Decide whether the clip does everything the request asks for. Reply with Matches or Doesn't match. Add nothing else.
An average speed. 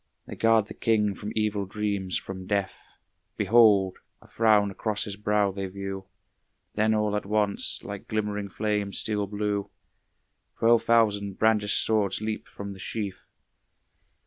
Matches